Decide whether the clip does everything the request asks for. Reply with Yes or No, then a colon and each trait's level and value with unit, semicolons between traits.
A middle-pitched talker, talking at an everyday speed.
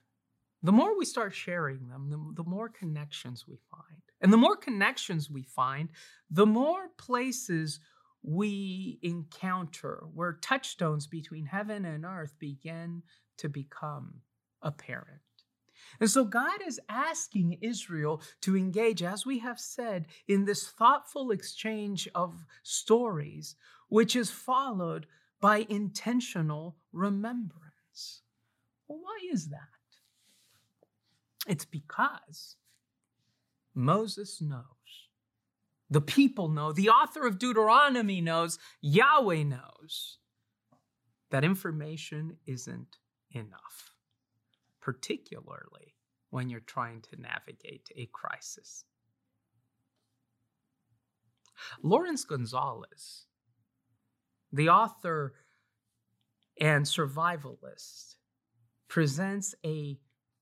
No: medium, 160 Hz; slow, 95 wpm